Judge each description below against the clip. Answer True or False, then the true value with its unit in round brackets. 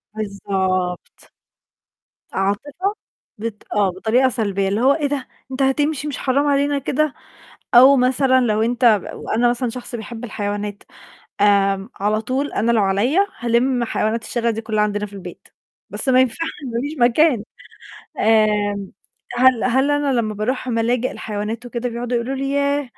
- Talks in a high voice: True (235 Hz)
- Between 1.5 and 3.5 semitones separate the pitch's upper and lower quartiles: False (3.9 semitones)